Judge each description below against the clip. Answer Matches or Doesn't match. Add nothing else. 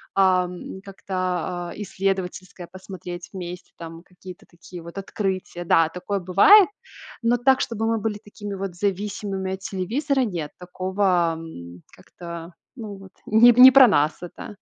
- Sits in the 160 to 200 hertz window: Matches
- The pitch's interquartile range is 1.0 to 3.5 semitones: Matches